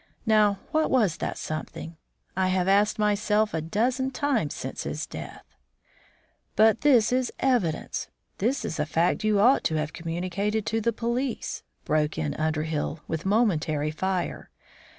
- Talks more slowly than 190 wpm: Yes, average, 150 wpm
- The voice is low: No, high, 200 Hz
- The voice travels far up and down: Yes, wide, 6.0 semitones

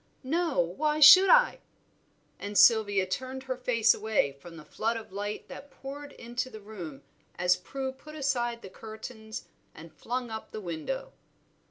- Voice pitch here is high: Yes, high, 230 Hz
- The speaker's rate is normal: Yes, average, 160 wpm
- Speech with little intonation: No, average, 4.9 semitones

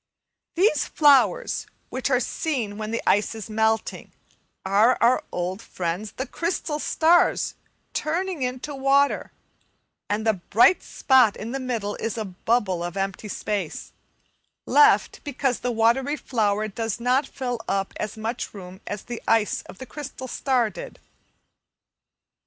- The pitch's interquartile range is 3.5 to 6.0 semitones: Yes, average, 4.5 semitones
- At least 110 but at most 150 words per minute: Yes, average, 140 wpm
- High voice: Yes, high, 230 Hz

